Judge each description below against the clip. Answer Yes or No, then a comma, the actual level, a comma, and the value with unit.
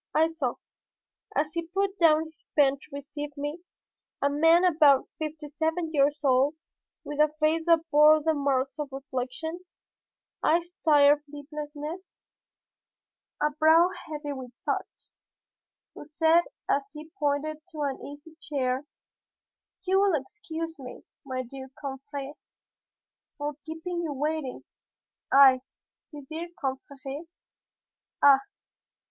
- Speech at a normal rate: No, slow, 125 wpm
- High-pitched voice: Yes, very high, 300 Hz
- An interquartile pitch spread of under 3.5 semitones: Yes, narrow, 2.4 semitones